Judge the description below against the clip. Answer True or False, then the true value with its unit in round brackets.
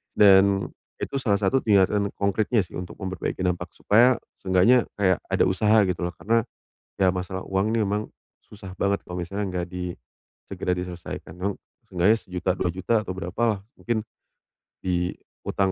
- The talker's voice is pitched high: False (95 Hz)